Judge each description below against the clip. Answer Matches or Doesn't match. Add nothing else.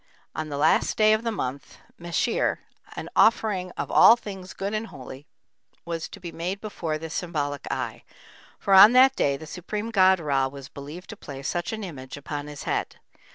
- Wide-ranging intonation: Matches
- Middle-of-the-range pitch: Matches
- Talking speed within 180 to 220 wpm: Matches